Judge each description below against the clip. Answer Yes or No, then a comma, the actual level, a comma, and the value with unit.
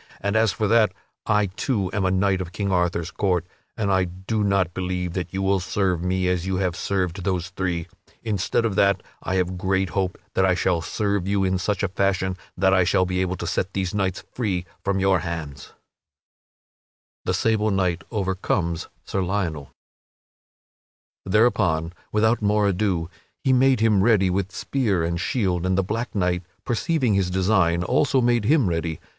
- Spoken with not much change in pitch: Yes, narrow, 2.2 semitones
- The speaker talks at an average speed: Yes, average, 180 wpm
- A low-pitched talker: Yes, very low, 95 Hz